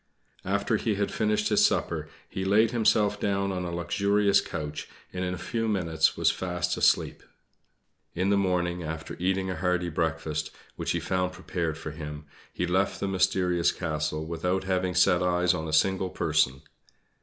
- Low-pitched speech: Yes, very low, 90 Hz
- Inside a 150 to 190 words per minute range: Yes, average, 170 wpm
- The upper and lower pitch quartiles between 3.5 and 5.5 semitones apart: No, average, 2.7 semitones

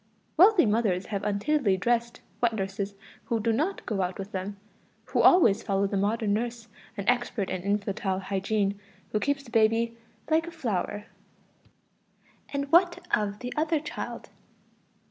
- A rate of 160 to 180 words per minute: No, average, 150 wpm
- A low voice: No, high, 220 Hz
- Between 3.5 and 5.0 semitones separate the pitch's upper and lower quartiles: Yes, average, 3.8 semitones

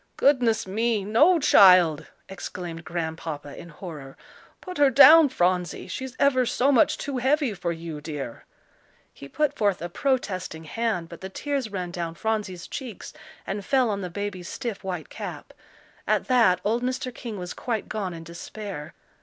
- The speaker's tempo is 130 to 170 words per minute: Yes, average, 160 wpm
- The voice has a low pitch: No, high, 195 Hz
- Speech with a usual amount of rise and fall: No, wide, 6.4 semitones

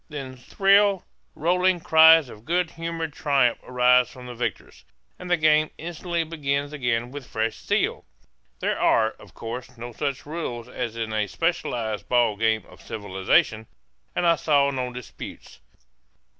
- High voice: No, low, 135 Hz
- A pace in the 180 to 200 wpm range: No, average, 150 wpm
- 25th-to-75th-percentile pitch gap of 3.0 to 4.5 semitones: No, wide, 5.6 semitones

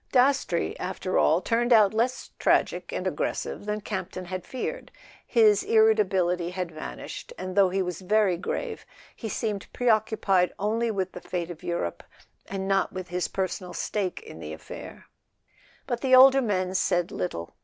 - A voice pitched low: No, high, 195 Hz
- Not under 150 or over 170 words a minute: Yes, average, 160 wpm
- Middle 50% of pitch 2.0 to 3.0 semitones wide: No, average, 3.8 semitones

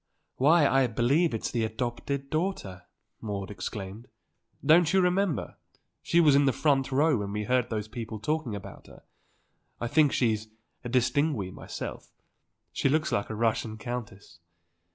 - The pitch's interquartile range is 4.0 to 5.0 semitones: No, wide, 5.5 semitones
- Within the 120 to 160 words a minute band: Yes, average, 150 wpm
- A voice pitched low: Yes, low, 125 Hz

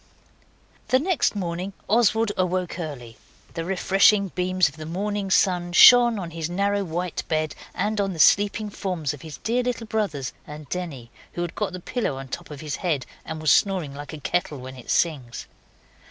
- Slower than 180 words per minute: No, average, 185 wpm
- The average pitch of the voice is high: No, medium, 180 Hz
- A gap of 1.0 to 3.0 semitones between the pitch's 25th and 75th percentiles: No, average, 4.7 semitones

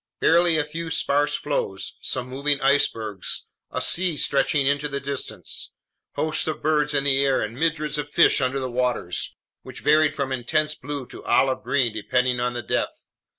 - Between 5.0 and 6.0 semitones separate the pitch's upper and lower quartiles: No, average, 2.9 semitones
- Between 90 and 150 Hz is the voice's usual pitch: Yes, medium, 140 Hz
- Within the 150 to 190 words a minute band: Yes, average, 175 wpm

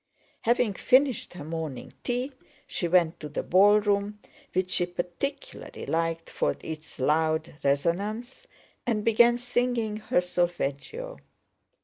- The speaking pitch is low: No, high, 190 Hz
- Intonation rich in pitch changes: Yes, wide, 6.4 semitones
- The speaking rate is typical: No, slow, 115 wpm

